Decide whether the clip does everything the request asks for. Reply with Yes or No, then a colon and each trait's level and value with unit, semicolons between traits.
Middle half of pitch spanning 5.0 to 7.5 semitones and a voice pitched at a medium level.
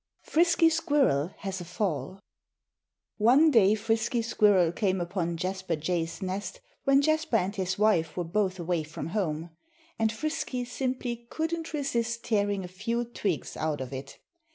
No: average, 5.3 semitones; high, 205 Hz